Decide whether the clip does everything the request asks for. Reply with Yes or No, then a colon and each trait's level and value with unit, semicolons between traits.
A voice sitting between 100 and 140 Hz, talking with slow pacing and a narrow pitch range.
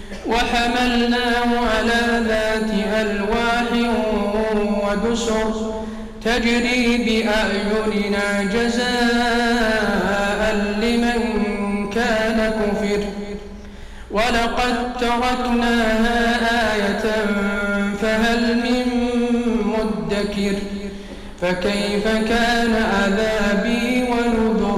No: high, 220 Hz; slow, 50 wpm; narrow, 2.3 semitones